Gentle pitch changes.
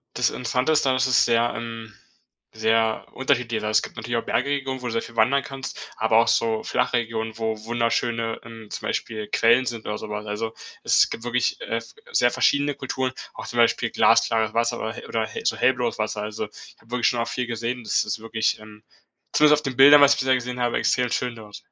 Yes: narrow, 2.1 semitones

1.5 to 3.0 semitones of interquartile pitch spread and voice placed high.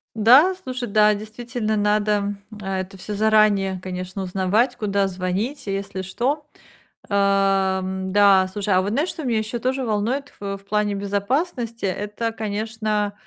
Yes: average, 2.7 semitones; high, 210 Hz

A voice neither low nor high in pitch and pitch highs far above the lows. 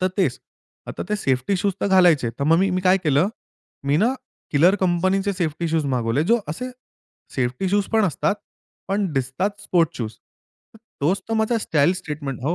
Yes: medium, 170 Hz; wide, 5.7 semitones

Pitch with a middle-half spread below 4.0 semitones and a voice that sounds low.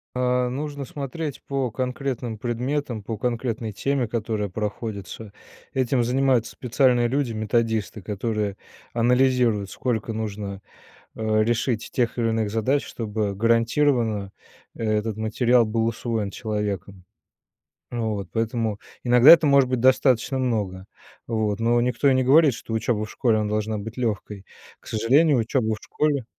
Yes: average, 2.9 semitones; low, 115 Hz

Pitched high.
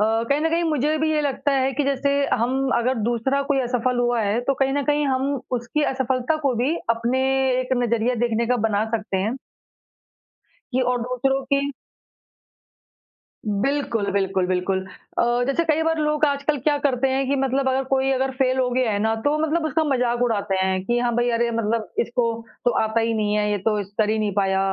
Yes: very high, 250 Hz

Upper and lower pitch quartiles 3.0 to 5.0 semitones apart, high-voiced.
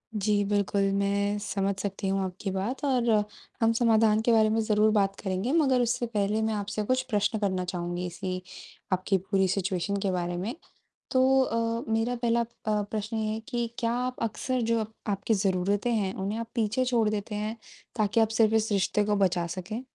No: narrow, 2.6 semitones; high, 210 Hz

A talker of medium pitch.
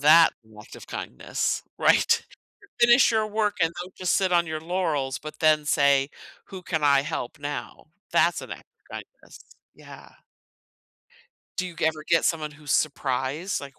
Yes: medium, 155 Hz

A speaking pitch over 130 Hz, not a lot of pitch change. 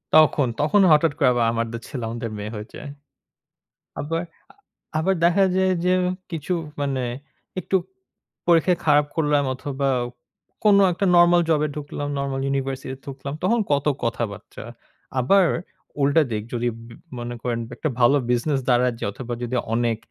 No: medium, 140 Hz; average, 5.1 semitones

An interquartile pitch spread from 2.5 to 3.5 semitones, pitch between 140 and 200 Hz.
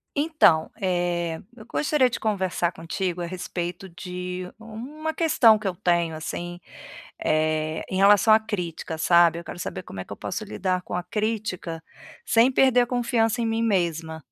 No: average, 4.7 semitones; medium, 185 Hz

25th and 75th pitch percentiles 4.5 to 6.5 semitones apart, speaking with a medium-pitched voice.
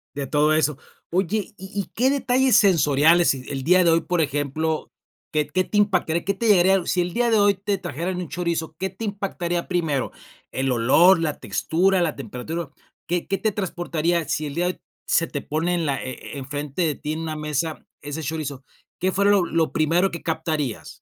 No: average, 3.8 semitones; medium, 170 Hz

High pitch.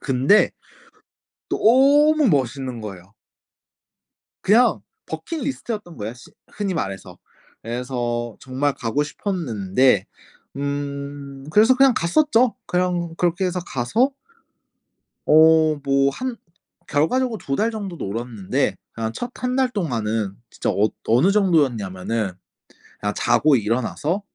No: medium, 145 Hz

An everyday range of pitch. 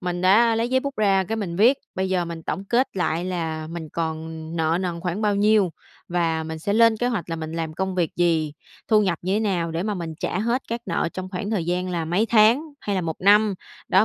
Yes: average, 4.2 semitones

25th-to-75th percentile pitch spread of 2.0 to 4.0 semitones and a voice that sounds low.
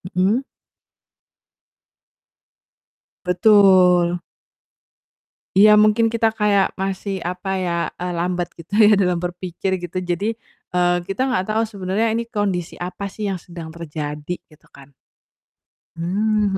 No: average, 2.9 semitones; medium, 185 Hz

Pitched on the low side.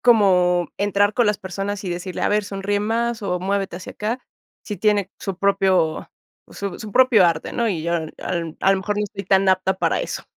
No: high, 195 Hz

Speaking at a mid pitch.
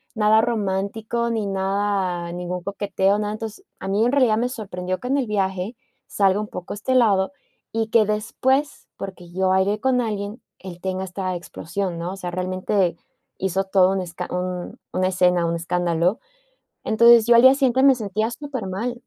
No: high, 200 Hz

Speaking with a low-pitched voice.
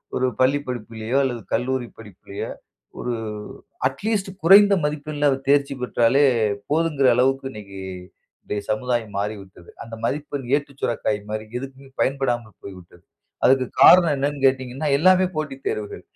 Yes: low, 130 Hz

